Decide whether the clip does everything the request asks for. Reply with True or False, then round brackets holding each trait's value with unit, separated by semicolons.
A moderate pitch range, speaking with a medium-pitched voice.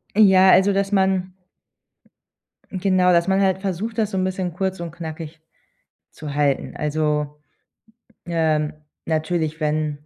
True (3.5 semitones; 175 Hz)